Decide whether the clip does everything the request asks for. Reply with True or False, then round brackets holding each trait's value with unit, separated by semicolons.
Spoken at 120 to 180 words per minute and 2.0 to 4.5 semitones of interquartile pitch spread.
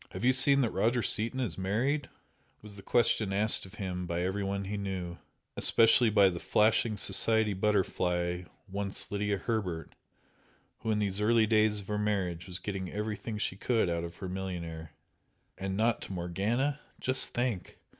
True (170 wpm; 2.9 semitones)